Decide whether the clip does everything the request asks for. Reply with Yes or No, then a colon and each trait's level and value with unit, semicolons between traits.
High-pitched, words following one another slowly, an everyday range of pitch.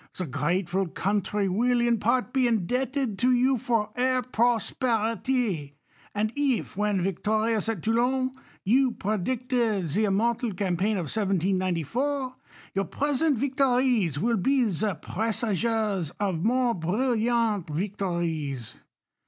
Yes: high, 220 Hz; slow, 120 wpm; average, 4.6 semitones